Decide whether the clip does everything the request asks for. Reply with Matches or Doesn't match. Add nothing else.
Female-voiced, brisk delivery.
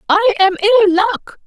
Doesn't match